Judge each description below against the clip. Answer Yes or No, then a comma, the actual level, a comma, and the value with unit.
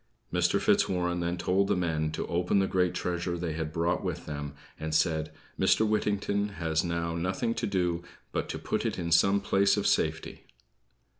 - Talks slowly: No, average, 180 wpm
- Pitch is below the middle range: Yes, very low, 90 Hz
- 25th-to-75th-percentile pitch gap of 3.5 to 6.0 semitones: No, average, 2.7 semitones